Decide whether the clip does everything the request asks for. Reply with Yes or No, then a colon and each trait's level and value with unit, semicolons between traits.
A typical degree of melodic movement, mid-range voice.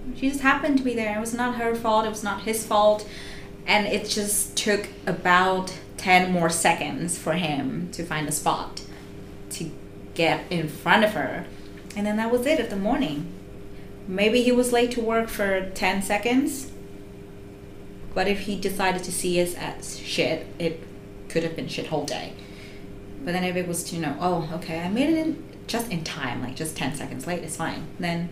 No: wide, 6.6 semitones; medium, 180 Hz